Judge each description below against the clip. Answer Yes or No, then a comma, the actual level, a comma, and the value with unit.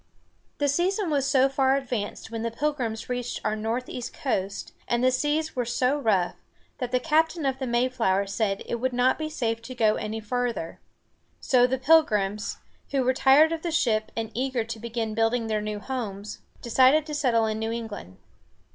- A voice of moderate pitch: No, high, 245 Hz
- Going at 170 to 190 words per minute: Yes, average, 185 wpm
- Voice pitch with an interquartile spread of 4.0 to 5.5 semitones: No, average, 3.4 semitones